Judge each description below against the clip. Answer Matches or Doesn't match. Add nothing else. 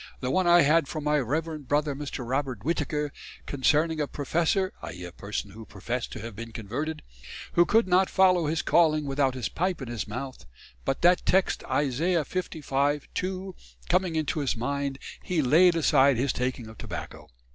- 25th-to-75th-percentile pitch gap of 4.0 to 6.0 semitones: Matches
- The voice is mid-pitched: Matches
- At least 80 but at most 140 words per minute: Doesn't match